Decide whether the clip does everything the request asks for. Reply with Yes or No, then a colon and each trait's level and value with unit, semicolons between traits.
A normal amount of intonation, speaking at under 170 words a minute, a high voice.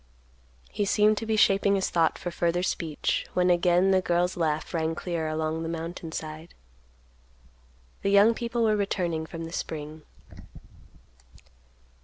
No: average, 3.5 semitones; average, 145 wpm; medium, 175 Hz